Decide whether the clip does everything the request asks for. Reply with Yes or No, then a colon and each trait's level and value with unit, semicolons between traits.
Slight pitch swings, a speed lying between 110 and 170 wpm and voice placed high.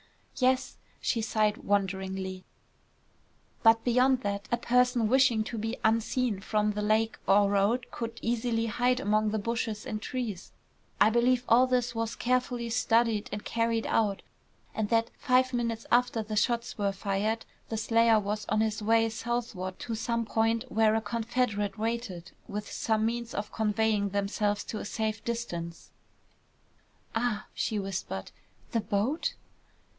Yes: narrow, 2.2 semitones; average, 150 wpm; high, 225 Hz